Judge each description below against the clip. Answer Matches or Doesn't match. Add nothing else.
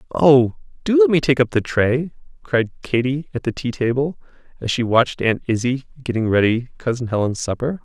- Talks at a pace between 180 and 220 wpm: Matches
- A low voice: Matches